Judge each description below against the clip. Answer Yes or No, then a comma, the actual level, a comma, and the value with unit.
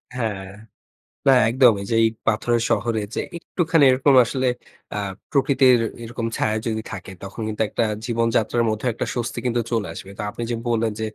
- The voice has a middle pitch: No, low, 115 Hz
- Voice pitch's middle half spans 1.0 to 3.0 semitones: Yes, narrow, 2.6 semitones